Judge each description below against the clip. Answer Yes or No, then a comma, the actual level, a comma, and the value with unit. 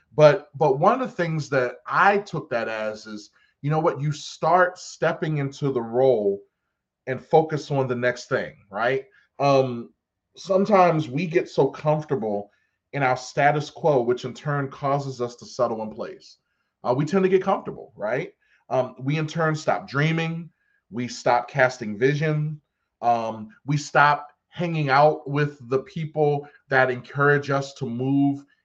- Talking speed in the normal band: Yes, average, 160 wpm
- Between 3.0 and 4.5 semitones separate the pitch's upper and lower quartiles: Yes, average, 3.5 semitones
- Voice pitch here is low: No, medium, 145 Hz